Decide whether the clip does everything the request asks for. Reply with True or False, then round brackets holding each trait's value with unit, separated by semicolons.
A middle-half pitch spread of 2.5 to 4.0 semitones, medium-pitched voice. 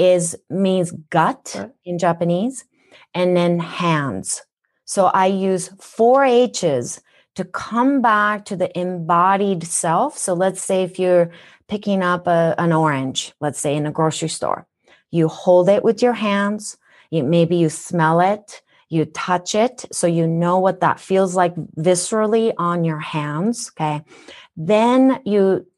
True (3.4 semitones; 180 Hz)